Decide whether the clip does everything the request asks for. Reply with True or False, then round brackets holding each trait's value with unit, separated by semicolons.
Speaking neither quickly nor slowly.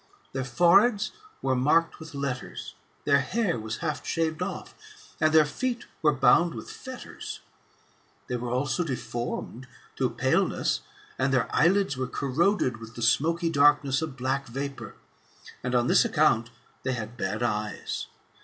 True (145 wpm)